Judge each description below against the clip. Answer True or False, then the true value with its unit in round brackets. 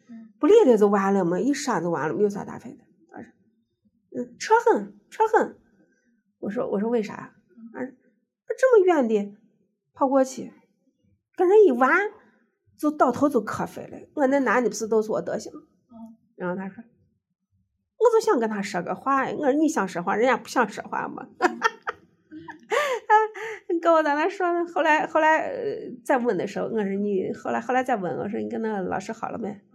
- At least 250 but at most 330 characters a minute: True (255 characters per minute)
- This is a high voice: True (250 Hz)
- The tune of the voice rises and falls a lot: True (7.4 semitones)